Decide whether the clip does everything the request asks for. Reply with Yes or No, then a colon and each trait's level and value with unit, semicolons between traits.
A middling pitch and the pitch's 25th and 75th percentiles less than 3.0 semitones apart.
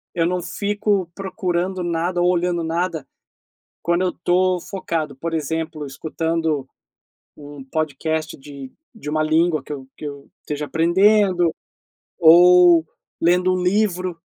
Yes: medium, 170 Hz; narrow, 2.6 semitones